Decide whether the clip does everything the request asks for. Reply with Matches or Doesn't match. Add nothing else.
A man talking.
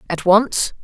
Doesn't match